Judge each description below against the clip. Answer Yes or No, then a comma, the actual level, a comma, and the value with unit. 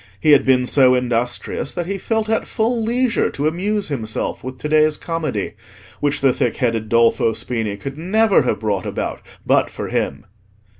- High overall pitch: No, medium, 140 Hz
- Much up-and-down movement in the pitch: Yes, wide, 7.5 semitones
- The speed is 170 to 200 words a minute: Yes, average, 180 wpm